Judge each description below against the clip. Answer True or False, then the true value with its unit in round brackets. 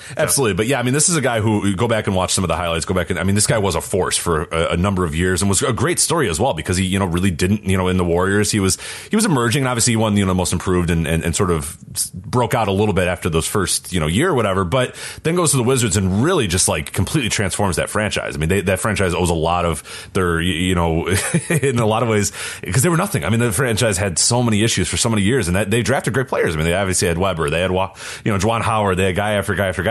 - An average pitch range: True (3.9 semitones)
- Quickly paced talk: True (315 wpm)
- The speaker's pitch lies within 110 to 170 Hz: False (100 Hz)